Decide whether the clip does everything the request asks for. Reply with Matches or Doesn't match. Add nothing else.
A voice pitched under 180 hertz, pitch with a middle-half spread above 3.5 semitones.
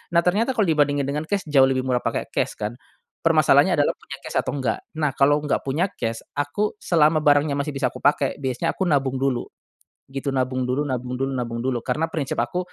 Doesn't match